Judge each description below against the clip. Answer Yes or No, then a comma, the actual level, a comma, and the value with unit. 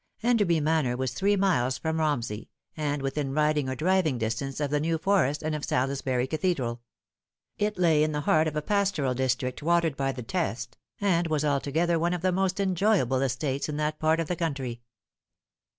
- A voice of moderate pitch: Yes, medium, 150 Hz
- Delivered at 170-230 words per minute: Yes, average, 185 wpm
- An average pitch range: Yes, average, 4.3 semitones